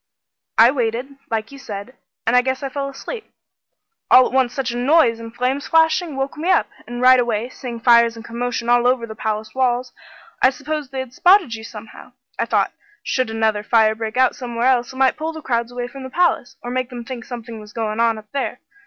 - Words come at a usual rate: No, fast, 225 wpm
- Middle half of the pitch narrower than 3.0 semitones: Yes, narrow, 2.5 semitones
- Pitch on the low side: No, high, 245 Hz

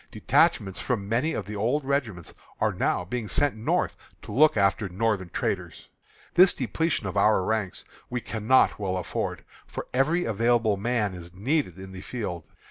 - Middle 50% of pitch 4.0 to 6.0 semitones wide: Yes, average, 4.5 semitones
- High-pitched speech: No, low, 110 Hz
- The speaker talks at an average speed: Yes, average, 165 wpm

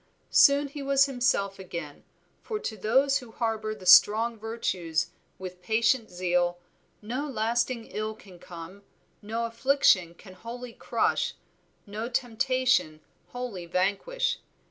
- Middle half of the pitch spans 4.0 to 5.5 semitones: Yes, average, 5.1 semitones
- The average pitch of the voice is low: No, high, 225 Hz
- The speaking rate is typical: No, slow, 120 wpm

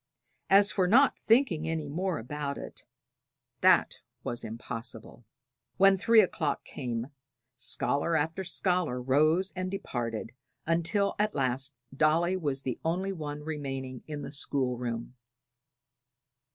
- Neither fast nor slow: No, slow, 125 wpm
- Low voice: No, medium, 150 Hz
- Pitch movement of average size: No, wide, 6.1 semitones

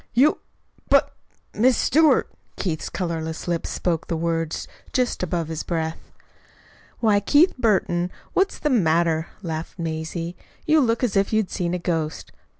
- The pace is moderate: Yes, average, 145 wpm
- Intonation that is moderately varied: No, wide, 5.7 semitones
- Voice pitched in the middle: Yes, medium, 175 Hz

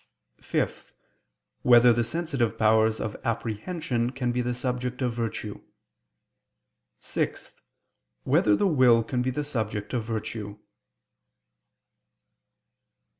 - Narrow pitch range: Yes, narrow, 2.3 semitones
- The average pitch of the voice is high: No, low, 120 Hz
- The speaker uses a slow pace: Yes, slow, 105 wpm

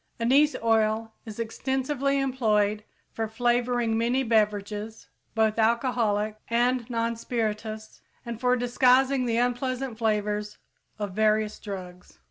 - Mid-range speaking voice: No, high, 230 Hz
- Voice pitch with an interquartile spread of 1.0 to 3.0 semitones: Yes, narrow, 2.5 semitones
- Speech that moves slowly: Yes, slow, 110 wpm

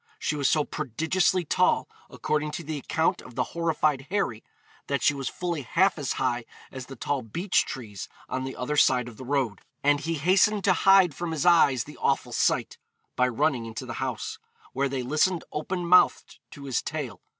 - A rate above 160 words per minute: Yes, average, 195 wpm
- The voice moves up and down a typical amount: Yes, average, 4.6 semitones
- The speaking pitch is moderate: Yes, medium, 145 Hz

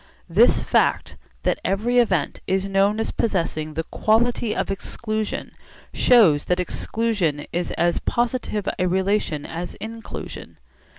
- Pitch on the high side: Yes, high, 195 Hz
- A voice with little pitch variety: No, average, 4.3 semitones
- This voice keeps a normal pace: No, slow, 125 wpm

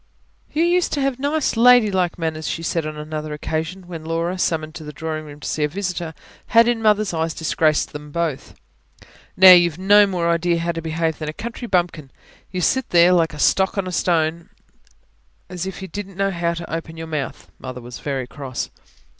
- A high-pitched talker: No, medium, 170 Hz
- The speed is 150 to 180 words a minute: No, average, 200 wpm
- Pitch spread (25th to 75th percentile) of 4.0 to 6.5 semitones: No, average, 3.4 semitones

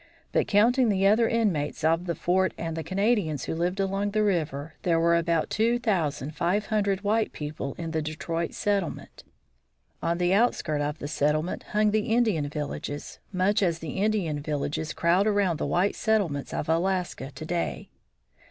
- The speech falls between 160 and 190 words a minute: Yes, average, 170 wpm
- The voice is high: No, medium, 175 Hz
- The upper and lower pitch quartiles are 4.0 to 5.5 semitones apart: Yes, average, 4.6 semitones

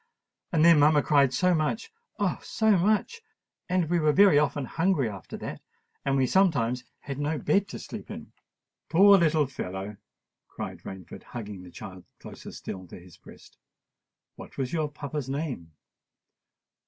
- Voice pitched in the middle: Yes, medium, 150 Hz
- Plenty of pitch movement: Yes, wide, 6.2 semitones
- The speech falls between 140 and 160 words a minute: Yes, average, 150 wpm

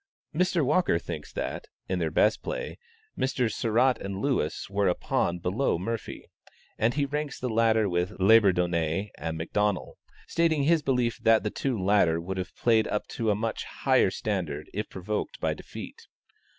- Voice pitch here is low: Yes, low, 105 Hz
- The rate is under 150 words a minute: No, average, 165 wpm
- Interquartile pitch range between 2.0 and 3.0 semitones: No, wide, 5.5 semitones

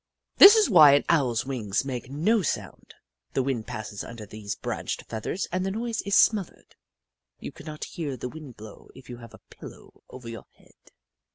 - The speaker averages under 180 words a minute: No, average, 185 wpm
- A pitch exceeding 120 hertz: Yes, low, 135 Hz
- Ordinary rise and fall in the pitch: No, wide, 6.8 semitones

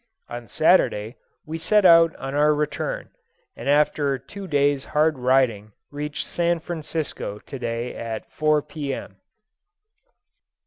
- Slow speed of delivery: Yes, slow, 125 wpm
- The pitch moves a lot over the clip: No, average, 3.9 semitones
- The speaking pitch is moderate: Yes, medium, 145 Hz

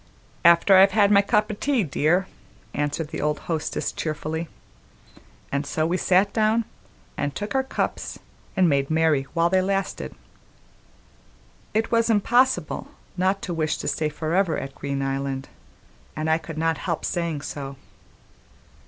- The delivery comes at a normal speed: Yes, average, 155 wpm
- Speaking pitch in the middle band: Yes, medium, 170 Hz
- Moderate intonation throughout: Yes, average, 4.7 semitones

